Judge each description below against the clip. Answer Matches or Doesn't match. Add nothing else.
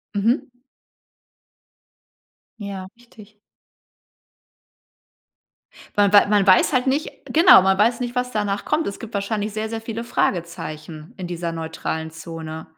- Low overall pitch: Doesn't match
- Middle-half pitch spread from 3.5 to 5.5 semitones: Matches